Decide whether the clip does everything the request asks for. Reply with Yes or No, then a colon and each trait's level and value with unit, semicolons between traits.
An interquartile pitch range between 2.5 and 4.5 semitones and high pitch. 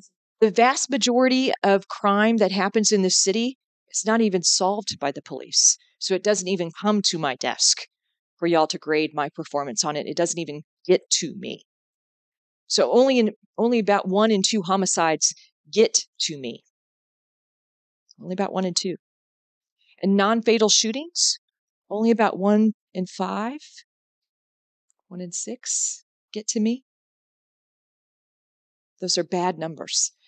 Yes: average, 4.1 semitones; high, 200 Hz